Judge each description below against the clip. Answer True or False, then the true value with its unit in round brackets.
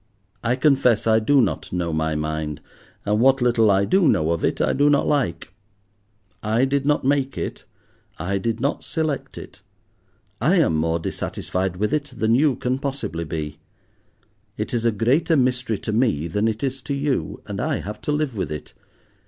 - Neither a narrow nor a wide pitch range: False (7.3 semitones)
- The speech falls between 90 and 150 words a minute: False (185 wpm)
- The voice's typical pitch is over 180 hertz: False (115 Hz)